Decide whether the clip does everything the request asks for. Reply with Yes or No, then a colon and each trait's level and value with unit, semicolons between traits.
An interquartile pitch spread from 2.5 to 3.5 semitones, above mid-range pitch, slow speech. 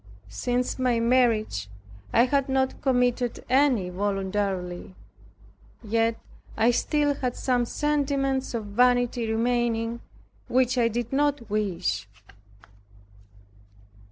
Yes: average, 3.2 semitones; high, 240 Hz; slow, 100 wpm